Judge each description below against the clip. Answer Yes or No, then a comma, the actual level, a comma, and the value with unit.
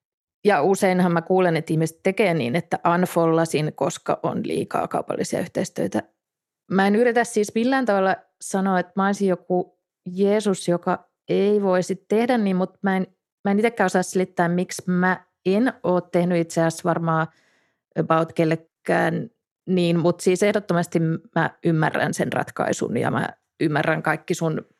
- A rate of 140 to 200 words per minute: Yes, average, 150 wpm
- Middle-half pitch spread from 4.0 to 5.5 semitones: No, narrow, 2.4 semitones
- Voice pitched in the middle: Yes, medium, 180 Hz